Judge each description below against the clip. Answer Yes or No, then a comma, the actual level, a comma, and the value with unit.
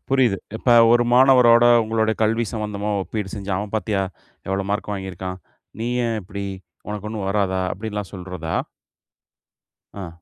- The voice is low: Yes, low, 105 Hz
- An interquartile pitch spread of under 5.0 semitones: Yes, average, 2.7 semitones